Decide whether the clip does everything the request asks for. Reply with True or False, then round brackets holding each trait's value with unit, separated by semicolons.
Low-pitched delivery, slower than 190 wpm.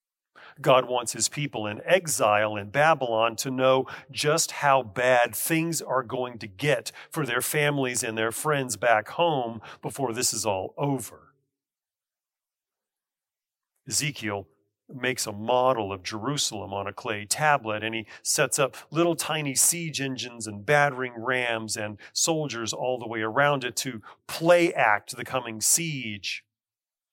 True (125 Hz; 145 wpm)